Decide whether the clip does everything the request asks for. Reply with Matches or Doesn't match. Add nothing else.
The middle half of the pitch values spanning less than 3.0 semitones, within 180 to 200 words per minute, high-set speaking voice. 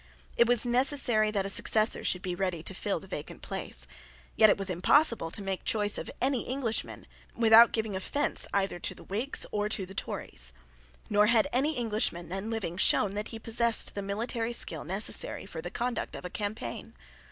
Doesn't match